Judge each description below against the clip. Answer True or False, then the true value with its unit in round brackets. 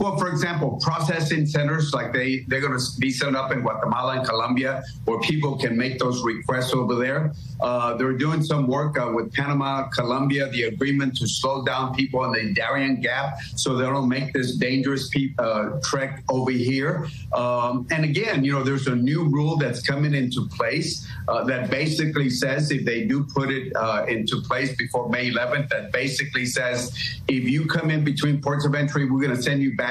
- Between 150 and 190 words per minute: False (200 wpm)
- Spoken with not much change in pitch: True (2.2 semitones)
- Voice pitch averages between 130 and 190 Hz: True (135 Hz)